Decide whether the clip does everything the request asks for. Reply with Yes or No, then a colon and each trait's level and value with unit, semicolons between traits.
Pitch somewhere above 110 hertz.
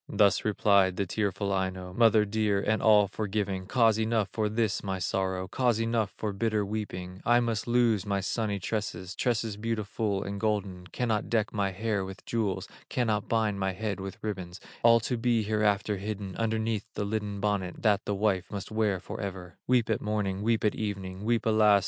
No: low, 105 Hz